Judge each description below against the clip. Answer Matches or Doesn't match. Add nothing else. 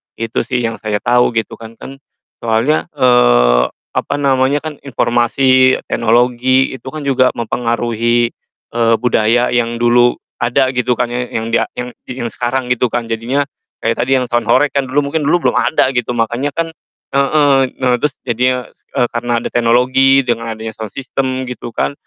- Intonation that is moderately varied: Doesn't match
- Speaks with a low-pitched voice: Matches